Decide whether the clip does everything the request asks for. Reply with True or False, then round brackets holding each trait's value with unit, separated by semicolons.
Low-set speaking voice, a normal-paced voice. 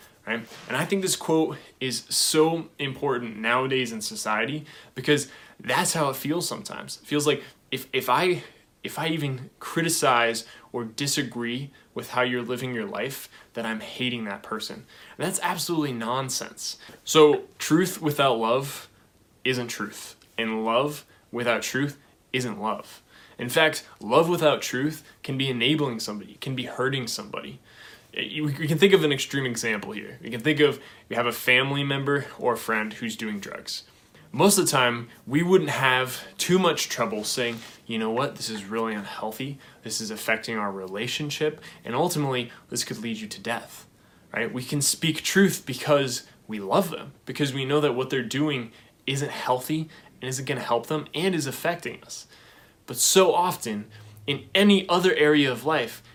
True (130 Hz; 170 wpm)